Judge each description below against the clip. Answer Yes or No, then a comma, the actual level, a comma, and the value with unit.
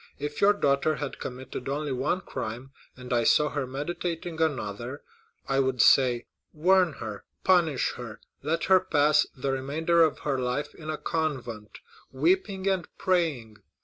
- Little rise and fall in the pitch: No, average, 4.3 semitones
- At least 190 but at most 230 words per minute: No, average, 150 wpm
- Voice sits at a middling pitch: Yes, medium, 145 Hz